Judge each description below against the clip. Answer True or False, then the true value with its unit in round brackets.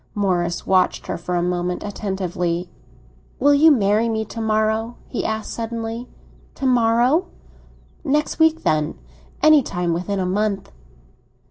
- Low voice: False (215 Hz)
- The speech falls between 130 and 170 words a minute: True (135 wpm)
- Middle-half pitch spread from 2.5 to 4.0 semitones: False (4.8 semitones)